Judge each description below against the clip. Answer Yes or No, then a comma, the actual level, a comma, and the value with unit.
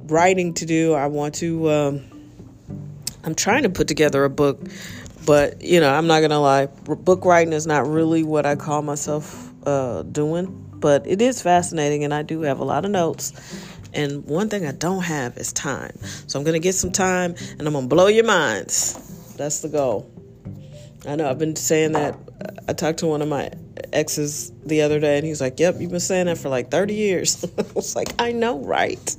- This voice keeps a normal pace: No, fast, 210 wpm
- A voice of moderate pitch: Yes, medium, 155 Hz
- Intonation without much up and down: No, average, 3.2 semitones